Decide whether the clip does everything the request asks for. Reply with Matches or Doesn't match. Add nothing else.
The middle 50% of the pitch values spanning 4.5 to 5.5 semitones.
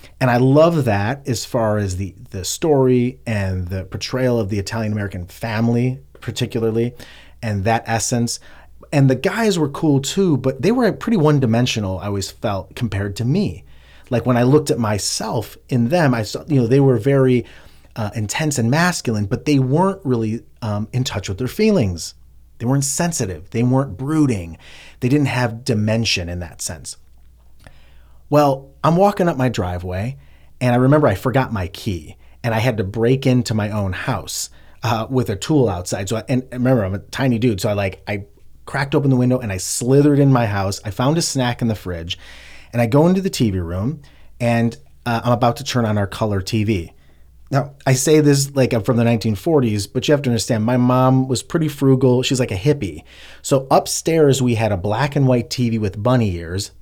Matches